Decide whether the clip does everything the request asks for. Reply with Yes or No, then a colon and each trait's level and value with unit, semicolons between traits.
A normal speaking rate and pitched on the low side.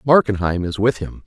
Yes: average, 190 wpm; low, 105 Hz